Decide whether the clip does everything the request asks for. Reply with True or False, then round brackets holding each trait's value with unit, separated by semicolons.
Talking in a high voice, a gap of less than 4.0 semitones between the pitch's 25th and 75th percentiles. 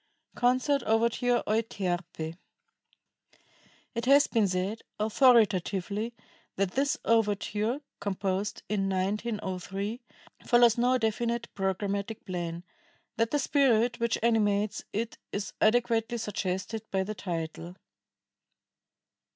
True (215 Hz; 3.4 semitones)